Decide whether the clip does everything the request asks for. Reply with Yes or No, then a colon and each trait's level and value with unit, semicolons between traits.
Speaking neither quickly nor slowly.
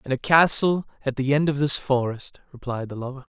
No: fast, 215 wpm